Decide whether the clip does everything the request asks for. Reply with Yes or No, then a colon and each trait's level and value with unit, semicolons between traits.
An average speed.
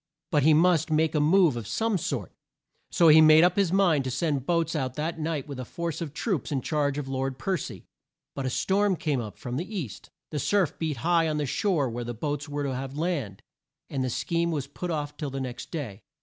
No: fast, 235 wpm